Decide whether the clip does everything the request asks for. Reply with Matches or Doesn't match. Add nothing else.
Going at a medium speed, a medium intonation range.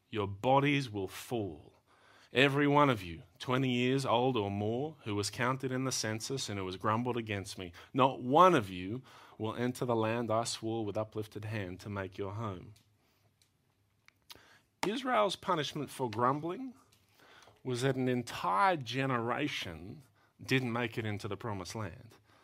Matches